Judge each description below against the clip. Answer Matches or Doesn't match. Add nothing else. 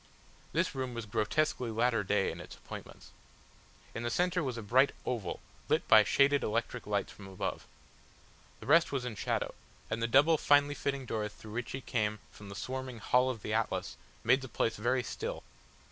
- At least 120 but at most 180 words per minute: Doesn't match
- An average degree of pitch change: Matches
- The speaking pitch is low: Matches